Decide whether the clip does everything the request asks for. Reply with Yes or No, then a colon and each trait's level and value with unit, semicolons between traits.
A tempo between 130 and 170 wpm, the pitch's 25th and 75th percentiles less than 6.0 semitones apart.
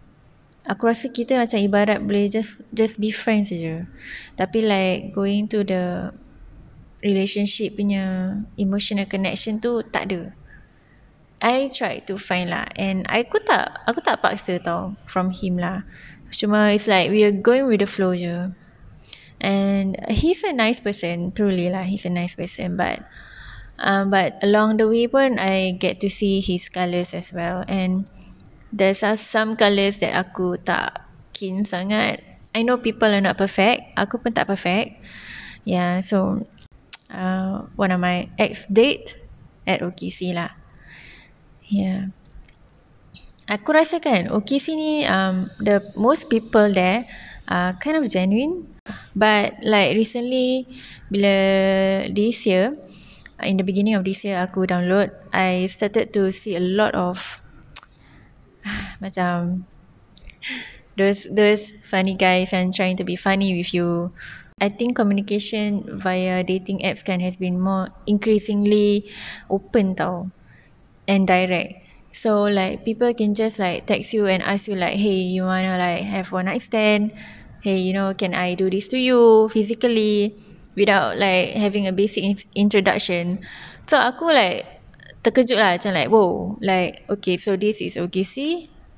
Yes: average, 150 wpm; narrow, 2.5 semitones